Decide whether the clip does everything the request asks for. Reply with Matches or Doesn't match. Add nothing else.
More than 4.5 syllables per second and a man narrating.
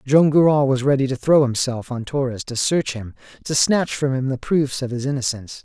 Matches